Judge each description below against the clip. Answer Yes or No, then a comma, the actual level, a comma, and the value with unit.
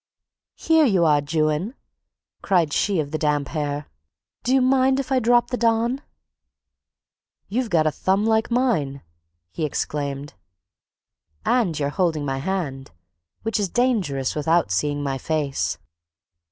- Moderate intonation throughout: No, wide, 8.2 semitones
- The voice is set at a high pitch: No, medium, 165 Hz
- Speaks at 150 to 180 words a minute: No, average, 140 wpm